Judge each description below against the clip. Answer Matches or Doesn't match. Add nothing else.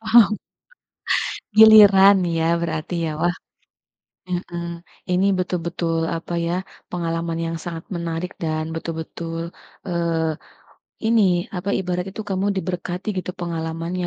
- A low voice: Doesn't match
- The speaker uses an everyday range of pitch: Doesn't match